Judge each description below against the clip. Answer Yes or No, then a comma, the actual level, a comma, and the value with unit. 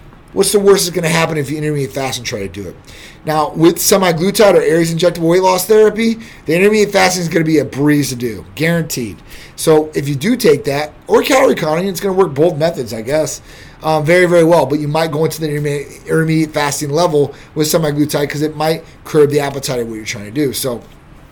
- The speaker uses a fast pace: Yes, fast, 230 wpm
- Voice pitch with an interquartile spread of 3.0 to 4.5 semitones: Yes, average, 3.3 semitones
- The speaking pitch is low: No, medium, 155 Hz